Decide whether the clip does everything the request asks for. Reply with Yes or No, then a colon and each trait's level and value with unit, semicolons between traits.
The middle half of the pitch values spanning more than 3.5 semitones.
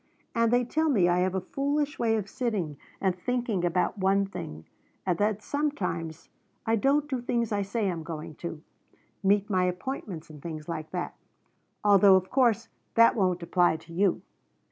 Yes: average, 4.8 semitones